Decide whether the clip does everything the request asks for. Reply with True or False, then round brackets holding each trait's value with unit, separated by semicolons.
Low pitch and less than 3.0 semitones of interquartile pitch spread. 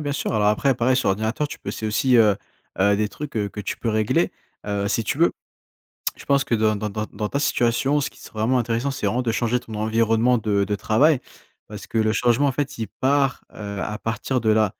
False (115 Hz; 3.4 semitones)